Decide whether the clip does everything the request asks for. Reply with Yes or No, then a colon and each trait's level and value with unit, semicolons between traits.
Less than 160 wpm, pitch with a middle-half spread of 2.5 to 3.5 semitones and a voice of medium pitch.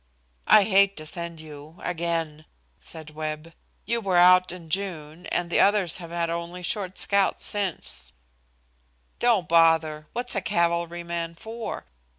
Yes: average, 145 wpm; average, 3.1 semitones; medium, 170 Hz